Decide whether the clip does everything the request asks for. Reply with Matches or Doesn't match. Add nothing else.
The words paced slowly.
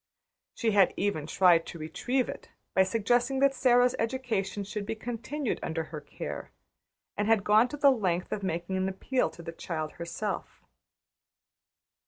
Doesn't match